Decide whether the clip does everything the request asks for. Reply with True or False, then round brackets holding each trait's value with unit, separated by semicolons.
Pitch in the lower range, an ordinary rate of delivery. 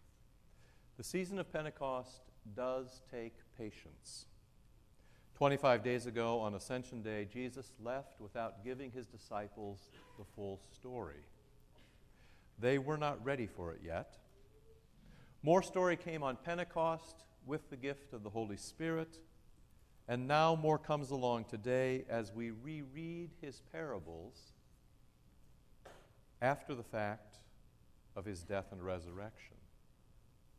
False (120 Hz; 120 wpm)